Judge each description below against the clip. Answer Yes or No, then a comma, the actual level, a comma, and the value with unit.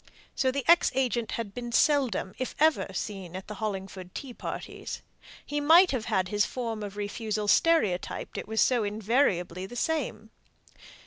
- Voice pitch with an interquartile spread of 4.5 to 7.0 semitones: Yes, average, 4.9 semitones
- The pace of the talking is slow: No, average, 165 wpm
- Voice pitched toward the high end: Yes, high, 220 Hz